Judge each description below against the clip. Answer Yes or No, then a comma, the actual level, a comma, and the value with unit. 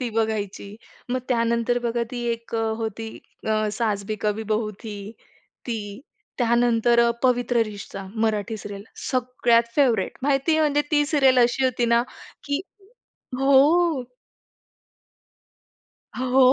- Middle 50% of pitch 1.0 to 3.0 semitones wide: Yes, average, 2.7 semitones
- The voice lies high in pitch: Yes, high, 235 Hz